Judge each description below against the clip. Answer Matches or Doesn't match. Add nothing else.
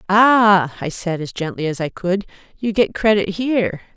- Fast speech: Doesn't match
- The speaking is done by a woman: Matches